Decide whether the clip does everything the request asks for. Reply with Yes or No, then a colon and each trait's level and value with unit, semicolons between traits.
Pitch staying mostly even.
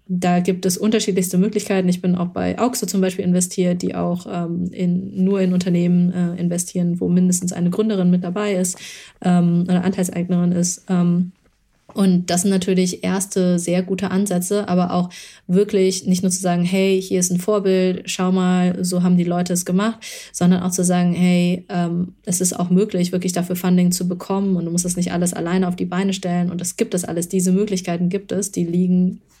Yes: narrow, 1.2 semitones